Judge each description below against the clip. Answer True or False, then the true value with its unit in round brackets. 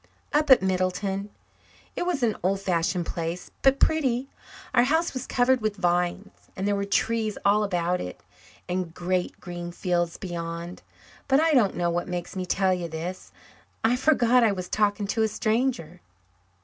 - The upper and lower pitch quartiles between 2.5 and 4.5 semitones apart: False (5.2 semitones)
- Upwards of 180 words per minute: False (170 wpm)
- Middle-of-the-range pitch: False (195 Hz)